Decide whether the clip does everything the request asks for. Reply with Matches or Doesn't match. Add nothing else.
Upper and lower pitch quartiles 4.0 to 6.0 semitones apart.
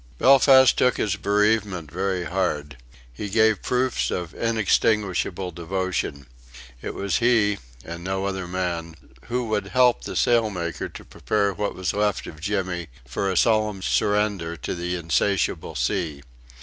Doesn't match